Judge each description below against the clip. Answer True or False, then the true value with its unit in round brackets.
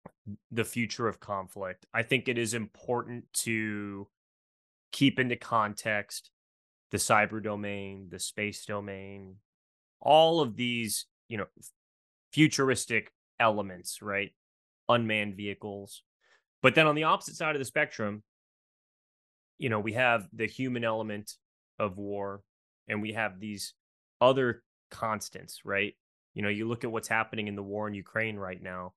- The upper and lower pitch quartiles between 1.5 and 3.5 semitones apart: True (3.0 semitones)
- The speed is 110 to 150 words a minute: True (140 wpm)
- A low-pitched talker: True (105 Hz)